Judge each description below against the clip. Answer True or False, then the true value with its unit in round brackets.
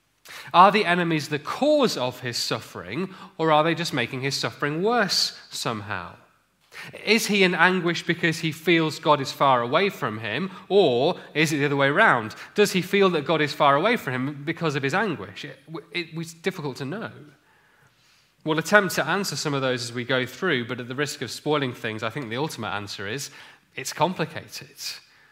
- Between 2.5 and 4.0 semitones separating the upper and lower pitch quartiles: False (4.9 semitones)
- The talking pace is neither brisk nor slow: True (195 wpm)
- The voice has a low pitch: False (155 Hz)